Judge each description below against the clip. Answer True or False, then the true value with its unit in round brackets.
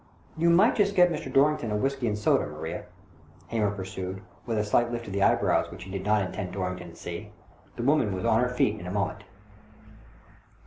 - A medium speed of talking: False (215 wpm)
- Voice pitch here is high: False (105 Hz)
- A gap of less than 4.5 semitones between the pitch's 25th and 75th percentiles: False (4.8 semitones)